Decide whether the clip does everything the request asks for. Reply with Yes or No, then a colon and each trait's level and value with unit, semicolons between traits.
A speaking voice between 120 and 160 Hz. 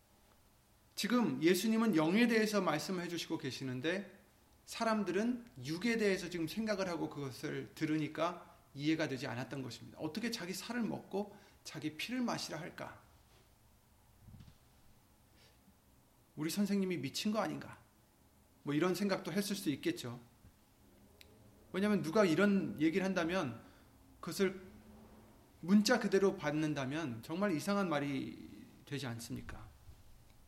No: medium, 170 Hz